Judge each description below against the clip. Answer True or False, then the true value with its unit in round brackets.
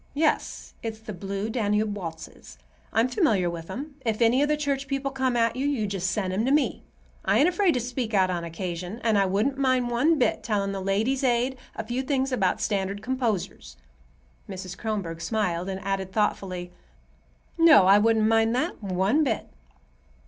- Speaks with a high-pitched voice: True (220 Hz)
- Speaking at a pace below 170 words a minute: False (185 wpm)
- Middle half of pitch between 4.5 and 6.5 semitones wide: True (5.1 semitones)